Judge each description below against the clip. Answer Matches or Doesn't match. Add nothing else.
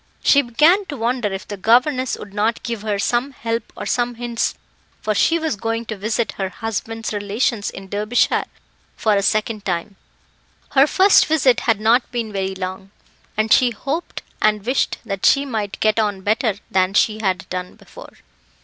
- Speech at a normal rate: Matches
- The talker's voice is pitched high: Matches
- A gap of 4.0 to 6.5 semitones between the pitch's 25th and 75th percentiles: Doesn't match